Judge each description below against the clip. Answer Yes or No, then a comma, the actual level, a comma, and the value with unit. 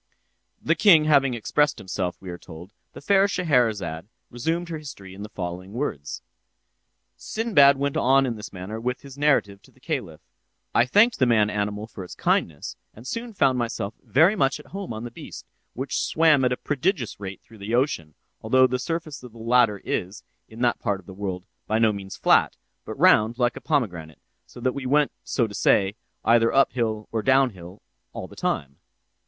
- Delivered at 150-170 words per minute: No, average, 185 wpm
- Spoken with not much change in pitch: No, wide, 5.6 semitones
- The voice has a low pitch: Yes, low, 120 Hz